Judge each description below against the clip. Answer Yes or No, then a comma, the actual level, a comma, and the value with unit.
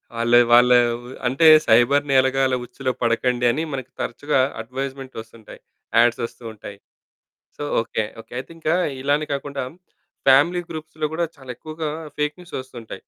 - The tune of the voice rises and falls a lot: No, average, 3.4 semitones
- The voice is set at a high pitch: No, low, 130 Hz